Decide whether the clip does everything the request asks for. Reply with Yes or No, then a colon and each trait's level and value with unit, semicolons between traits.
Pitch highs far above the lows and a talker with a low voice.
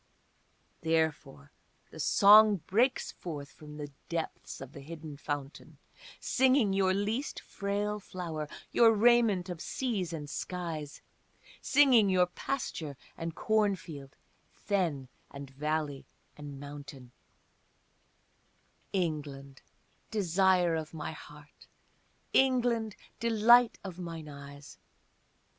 No: wide, 6.0 semitones; medium, 170 Hz